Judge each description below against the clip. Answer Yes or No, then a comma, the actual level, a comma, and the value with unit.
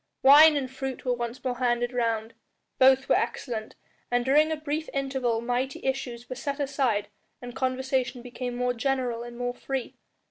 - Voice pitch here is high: Yes, very high, 255 Hz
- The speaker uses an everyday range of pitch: No, narrow, 1.8 semitones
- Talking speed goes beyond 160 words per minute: Yes, average, 170 wpm